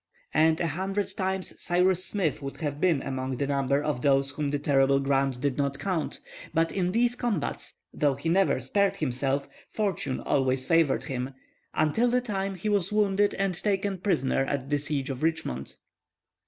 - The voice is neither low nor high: Yes, medium, 155 Hz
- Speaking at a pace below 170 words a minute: No, average, 175 wpm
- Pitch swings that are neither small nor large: No, wide, 5.8 semitones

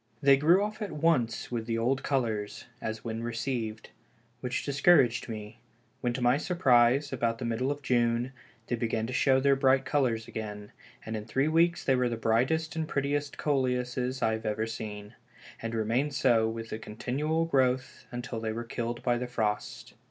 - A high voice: No, low, 125 Hz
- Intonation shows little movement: No, average, 3.3 semitones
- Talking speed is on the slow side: No, average, 185 wpm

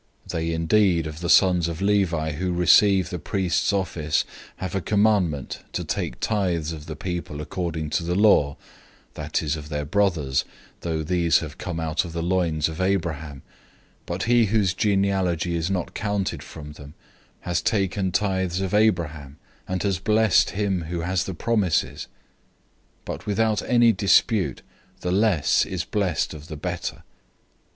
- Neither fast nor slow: Yes, average, 165 wpm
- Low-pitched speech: Yes, very low, 90 Hz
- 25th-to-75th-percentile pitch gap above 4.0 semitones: No, average, 3.6 semitones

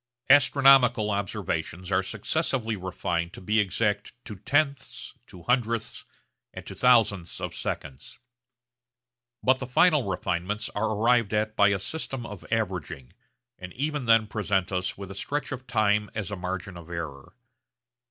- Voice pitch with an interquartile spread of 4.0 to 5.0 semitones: Yes, average, 4.7 semitones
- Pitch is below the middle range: Yes, low, 105 Hz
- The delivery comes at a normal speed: Yes, average, 145 wpm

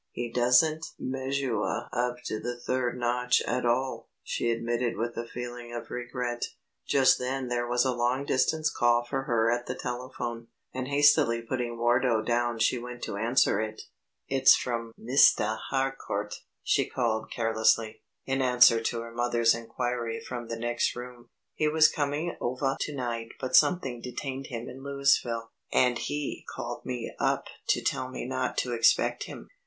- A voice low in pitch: Yes, low, 120 Hz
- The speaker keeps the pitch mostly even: Yes, narrow, 1.8 semitones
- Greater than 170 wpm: No, average, 165 wpm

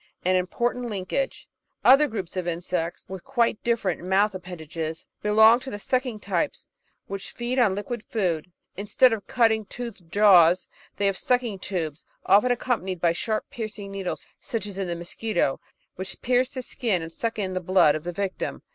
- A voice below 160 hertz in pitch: No, high, 200 Hz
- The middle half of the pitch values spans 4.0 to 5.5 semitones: Yes, average, 4.4 semitones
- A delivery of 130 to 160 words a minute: No, average, 175 wpm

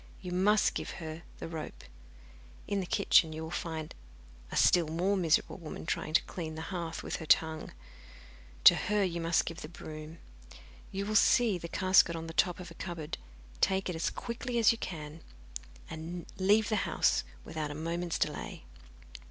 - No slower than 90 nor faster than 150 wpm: No, average, 180 wpm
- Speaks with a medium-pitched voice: Yes, medium, 170 Hz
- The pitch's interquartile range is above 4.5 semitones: No, average, 3.0 semitones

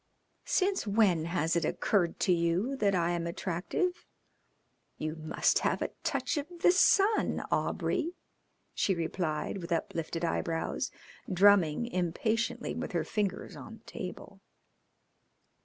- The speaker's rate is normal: No, slow, 125 wpm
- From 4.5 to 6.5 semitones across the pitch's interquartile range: Yes, average, 5.2 semitones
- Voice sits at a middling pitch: Yes, medium, 180 Hz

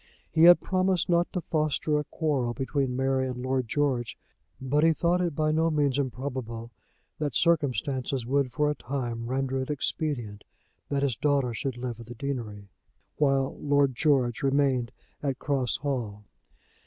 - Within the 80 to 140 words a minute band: No, average, 160 wpm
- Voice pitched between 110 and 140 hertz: Yes, low, 135 Hz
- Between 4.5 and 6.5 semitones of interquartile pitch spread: No, average, 3.1 semitones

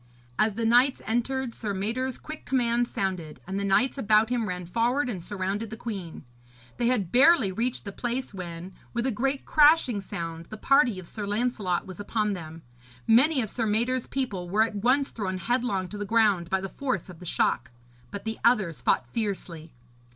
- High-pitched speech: Yes, high, 215 Hz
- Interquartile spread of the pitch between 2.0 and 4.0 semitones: No, average, 4.6 semitones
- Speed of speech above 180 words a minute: Yes, average, 190 wpm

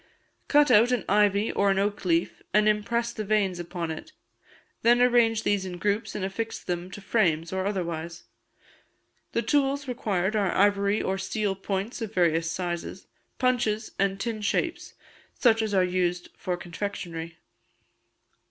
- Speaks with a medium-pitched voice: No, high, 200 Hz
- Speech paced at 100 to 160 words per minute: Yes, average, 150 wpm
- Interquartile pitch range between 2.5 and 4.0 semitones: Yes, average, 3.4 semitones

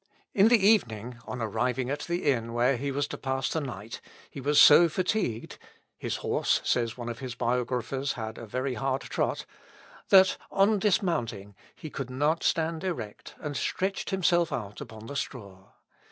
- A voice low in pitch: Yes, low, 130 Hz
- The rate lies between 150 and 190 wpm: Yes, average, 170 wpm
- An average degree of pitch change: No, wide, 6.0 semitones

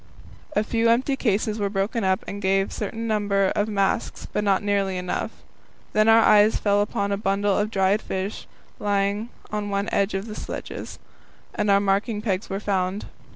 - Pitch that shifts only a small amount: Yes, narrow, 1.4 semitones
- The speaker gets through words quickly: No, average, 180 wpm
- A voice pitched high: Yes, high, 205 Hz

